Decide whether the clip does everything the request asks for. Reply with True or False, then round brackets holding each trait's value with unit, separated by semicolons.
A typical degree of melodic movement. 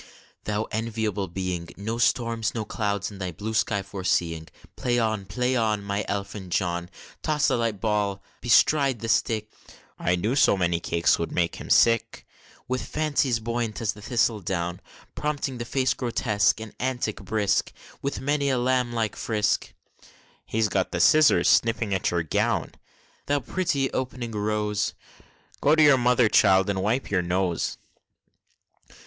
True (3.9 semitones)